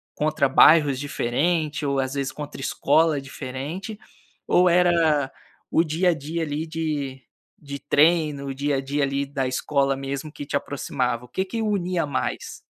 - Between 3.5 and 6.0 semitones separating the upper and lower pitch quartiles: No, average, 2.9 semitones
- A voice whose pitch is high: No, medium, 145 Hz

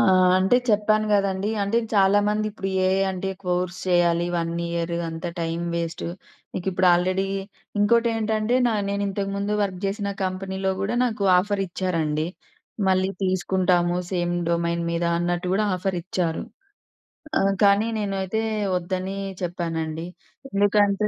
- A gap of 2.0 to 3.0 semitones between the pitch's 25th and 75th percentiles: Yes, narrow, 2.6 semitones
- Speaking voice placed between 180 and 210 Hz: Yes, high, 190 Hz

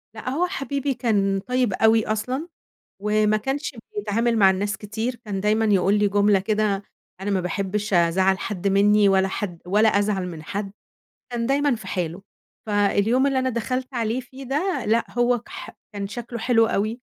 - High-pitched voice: Yes, high, 215 Hz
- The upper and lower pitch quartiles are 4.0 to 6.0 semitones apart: No, average, 3.5 semitones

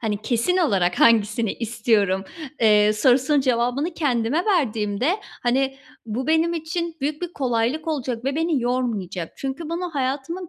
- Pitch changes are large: Yes, wide, 5.9 semitones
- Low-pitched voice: No, very high, 255 Hz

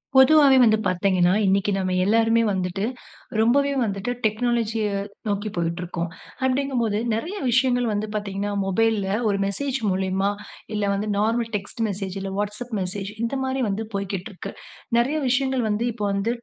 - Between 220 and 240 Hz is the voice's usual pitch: No, high, 210 Hz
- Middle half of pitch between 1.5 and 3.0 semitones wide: No, average, 3.6 semitones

